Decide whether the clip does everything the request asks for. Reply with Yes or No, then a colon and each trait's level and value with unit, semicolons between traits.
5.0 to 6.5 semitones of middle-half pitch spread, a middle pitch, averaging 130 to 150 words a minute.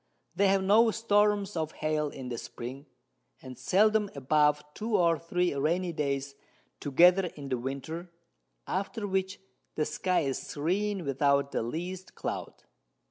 Yes: wide, 5.5 semitones; medium, 165 Hz; average, 140 wpm